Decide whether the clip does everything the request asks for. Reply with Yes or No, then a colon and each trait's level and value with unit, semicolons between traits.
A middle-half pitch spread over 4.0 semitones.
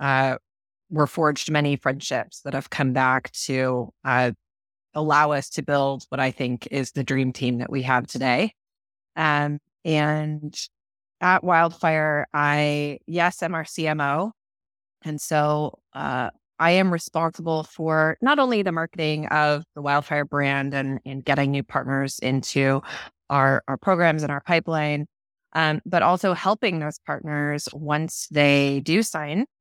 No: average, 2.9 semitones